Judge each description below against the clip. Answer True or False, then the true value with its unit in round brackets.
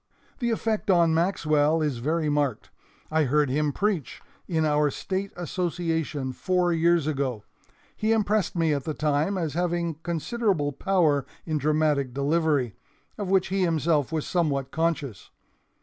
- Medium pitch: True (160 Hz)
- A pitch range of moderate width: True (3.4 semitones)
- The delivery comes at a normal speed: True (145 wpm)